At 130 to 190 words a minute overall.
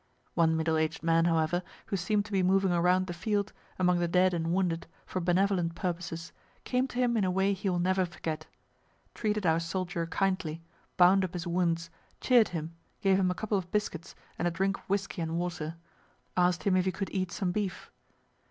No: average, 200 wpm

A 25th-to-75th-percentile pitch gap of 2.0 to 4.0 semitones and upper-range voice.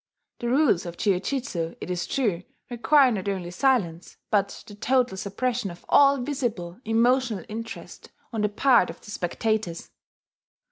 No: wide, 5.6 semitones; high, 215 Hz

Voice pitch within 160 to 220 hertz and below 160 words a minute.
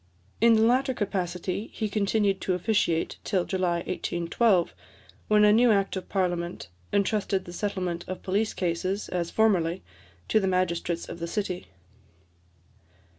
Yes: high, 190 Hz; average, 140 wpm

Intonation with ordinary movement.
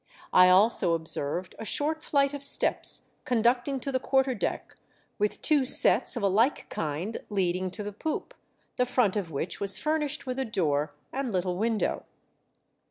No: wide, 6.5 semitones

